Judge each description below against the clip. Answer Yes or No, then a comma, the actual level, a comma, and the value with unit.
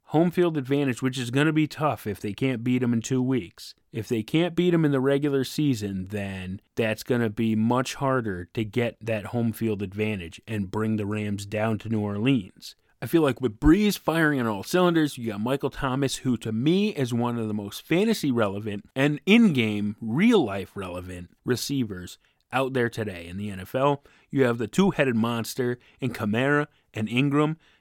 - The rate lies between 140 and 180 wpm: No, average, 190 wpm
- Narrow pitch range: No, average, 4.7 semitones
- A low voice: Yes, low, 120 Hz